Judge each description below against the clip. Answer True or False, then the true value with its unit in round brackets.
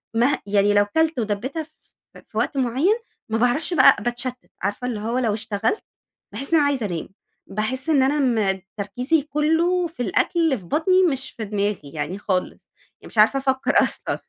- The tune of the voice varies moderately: False (6.1 semitones)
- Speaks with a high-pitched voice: True (245 Hz)